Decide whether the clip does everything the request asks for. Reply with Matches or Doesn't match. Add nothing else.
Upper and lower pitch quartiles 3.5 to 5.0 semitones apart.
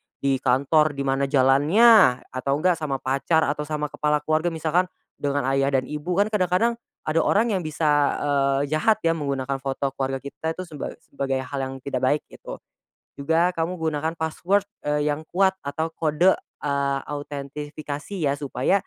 Doesn't match